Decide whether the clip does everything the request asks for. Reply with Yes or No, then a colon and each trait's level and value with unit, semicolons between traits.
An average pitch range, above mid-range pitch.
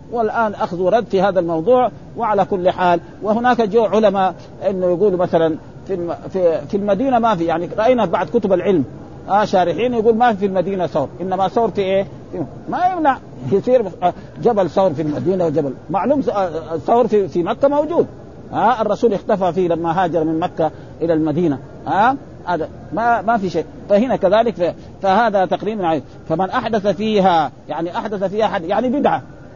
Yes: average, 4.9 semitones; high, 195 Hz